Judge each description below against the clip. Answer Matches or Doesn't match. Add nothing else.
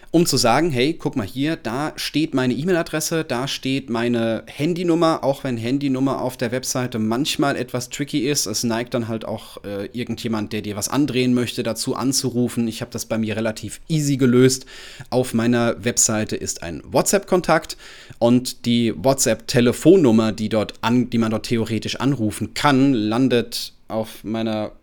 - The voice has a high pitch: Doesn't match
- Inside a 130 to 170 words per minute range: Matches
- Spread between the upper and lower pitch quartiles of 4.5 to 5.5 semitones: Doesn't match